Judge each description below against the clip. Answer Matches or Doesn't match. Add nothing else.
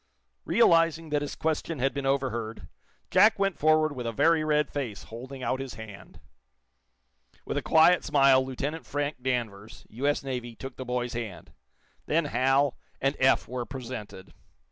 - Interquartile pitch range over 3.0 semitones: Matches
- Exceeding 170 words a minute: Doesn't match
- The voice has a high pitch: Doesn't match